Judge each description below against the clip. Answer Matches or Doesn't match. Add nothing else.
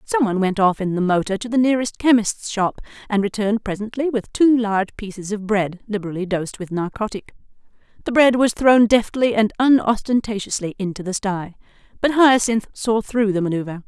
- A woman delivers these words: Matches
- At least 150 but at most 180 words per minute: Matches